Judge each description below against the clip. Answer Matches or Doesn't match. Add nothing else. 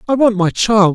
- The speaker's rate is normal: Doesn't match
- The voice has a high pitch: Matches